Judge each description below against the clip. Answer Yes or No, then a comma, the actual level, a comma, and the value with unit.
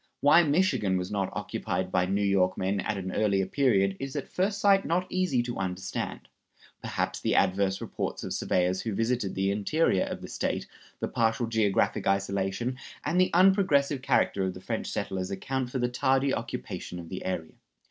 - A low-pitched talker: Yes, low, 105 Hz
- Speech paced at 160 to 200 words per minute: Yes, average, 180 wpm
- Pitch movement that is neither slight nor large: No, wide, 6.3 semitones